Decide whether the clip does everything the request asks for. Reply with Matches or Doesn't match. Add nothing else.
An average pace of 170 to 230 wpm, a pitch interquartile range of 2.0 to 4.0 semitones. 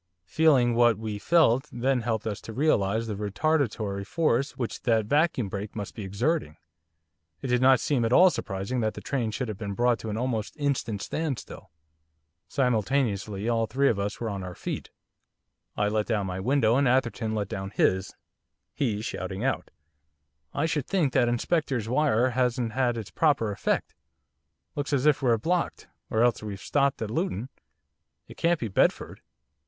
Doesn't match